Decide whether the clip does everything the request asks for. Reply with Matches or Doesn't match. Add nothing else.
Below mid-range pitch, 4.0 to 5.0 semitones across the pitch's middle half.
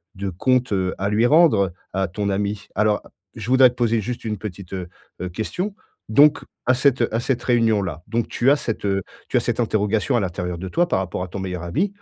Matches